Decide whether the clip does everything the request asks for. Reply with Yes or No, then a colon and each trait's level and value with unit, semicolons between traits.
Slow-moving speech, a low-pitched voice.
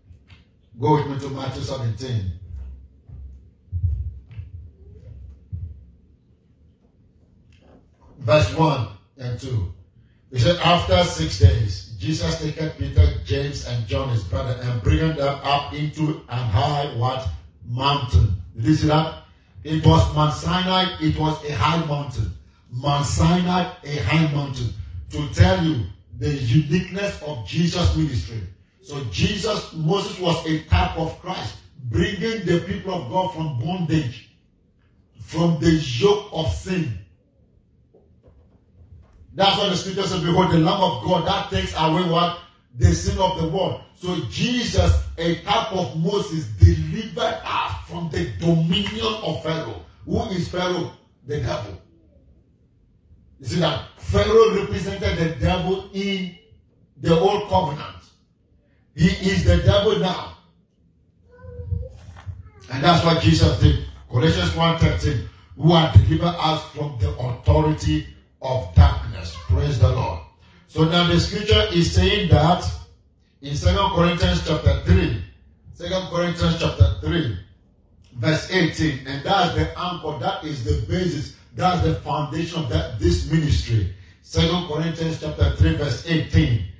Yes: slow, 130 wpm; low, 125 Hz